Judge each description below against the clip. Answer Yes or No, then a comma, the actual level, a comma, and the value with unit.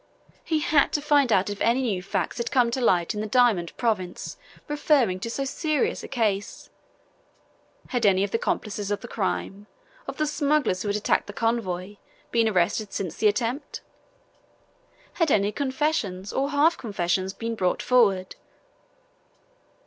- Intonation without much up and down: No, average, 5.2 semitones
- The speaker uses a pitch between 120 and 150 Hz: No, high, 225 Hz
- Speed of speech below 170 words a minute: Yes, average, 160 wpm